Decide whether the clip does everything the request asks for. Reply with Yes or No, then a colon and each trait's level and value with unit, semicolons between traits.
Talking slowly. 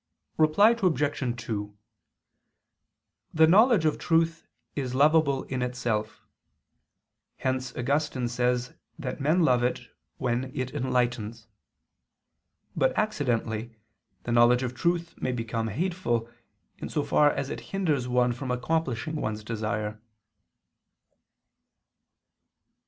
Yes: slow, 110 wpm